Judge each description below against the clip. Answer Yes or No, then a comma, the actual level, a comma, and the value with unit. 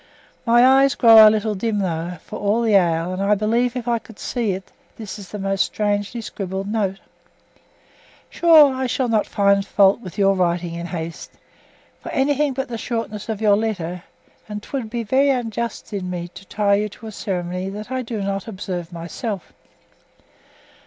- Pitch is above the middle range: Yes, high, 210 Hz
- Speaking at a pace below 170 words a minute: No, average, 180 wpm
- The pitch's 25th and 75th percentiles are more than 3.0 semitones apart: Yes, average, 3.6 semitones